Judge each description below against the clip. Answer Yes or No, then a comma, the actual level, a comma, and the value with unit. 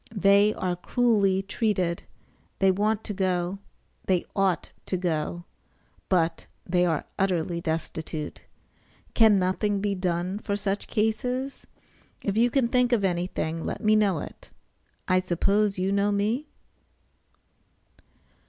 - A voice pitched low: No, high, 195 Hz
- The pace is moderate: No, slow, 125 wpm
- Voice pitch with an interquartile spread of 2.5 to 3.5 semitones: Yes, average, 3.0 semitones